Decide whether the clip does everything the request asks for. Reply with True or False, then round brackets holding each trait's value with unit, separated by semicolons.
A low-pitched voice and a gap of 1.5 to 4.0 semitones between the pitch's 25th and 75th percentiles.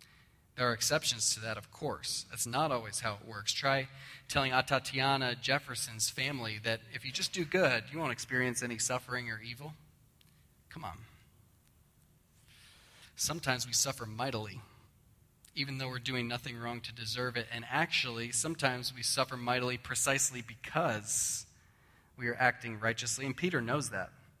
True (125 Hz; 2.7 semitones)